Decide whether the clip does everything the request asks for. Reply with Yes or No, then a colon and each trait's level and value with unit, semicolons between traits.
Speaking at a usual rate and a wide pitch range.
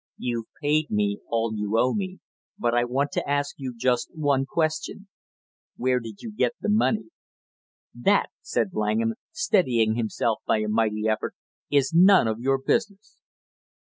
Yes: average, 155 wpm; wide, 6.0 semitones